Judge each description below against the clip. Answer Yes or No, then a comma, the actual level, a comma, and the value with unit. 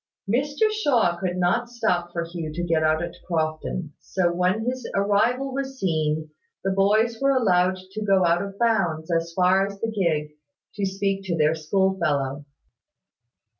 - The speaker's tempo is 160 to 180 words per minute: Yes, average, 170 wpm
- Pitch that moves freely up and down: No, average, 4.5 semitones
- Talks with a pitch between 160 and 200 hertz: Yes, high, 190 Hz